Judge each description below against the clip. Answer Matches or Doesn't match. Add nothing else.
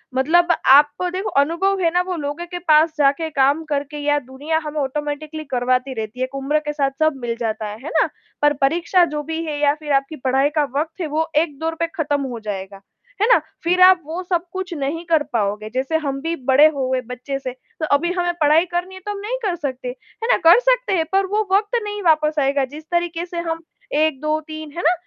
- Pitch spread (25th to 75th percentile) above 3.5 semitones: Matches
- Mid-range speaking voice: Doesn't match